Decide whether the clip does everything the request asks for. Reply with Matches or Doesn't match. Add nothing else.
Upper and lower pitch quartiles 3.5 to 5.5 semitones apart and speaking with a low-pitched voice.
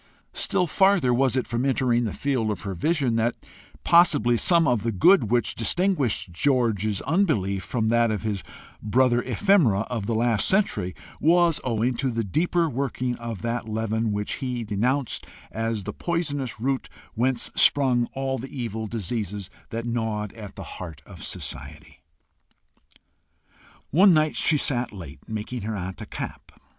Matches